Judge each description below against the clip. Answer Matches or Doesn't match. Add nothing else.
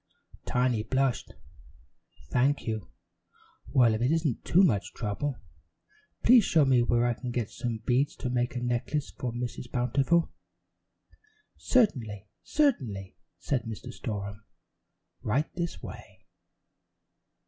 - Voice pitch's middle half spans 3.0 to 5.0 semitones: Matches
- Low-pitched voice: Matches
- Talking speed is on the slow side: Matches